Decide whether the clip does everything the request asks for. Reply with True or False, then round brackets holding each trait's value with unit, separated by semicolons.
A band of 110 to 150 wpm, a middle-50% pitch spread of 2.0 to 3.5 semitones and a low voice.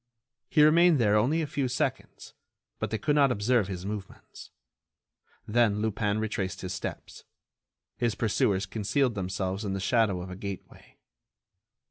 False (145 wpm; 4.3 semitones; 105 Hz)